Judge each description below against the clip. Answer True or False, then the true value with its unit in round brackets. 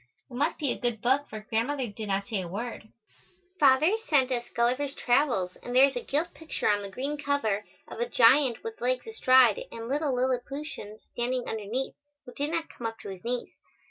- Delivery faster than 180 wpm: True (205 wpm)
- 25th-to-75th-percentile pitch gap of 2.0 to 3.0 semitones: False (3.8 semitones)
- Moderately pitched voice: False (245 Hz)